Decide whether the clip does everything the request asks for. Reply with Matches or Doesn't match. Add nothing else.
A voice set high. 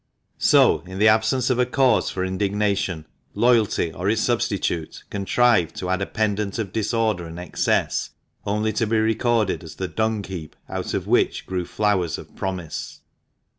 Doesn't match